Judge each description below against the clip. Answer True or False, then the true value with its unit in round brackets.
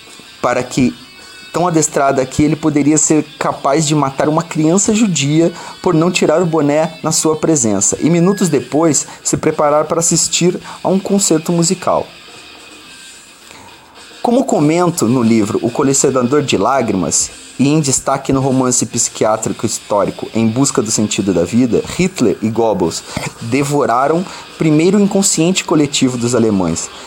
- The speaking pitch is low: False (155 Hz)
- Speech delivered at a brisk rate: False (140 wpm)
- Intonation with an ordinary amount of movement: True (4.6 semitones)